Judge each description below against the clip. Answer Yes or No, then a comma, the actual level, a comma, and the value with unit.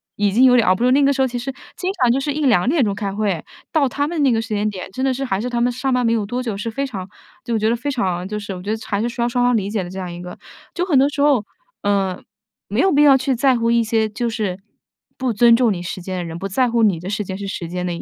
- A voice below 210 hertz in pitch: No, high, 230 Hz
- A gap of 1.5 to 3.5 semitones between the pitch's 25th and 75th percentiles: No, average, 4.6 semitones